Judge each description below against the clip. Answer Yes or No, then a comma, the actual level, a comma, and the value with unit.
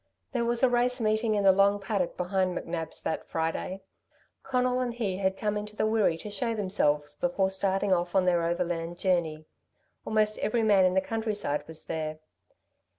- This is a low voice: No, high, 195 Hz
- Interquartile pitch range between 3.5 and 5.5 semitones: Yes, average, 3.8 semitones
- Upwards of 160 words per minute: Yes, average, 180 wpm